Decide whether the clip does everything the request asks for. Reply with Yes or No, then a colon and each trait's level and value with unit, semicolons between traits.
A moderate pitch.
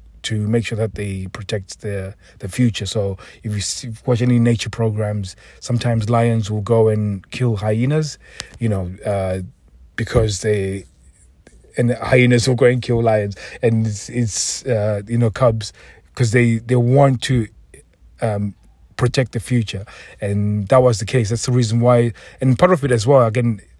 No: low, 115 Hz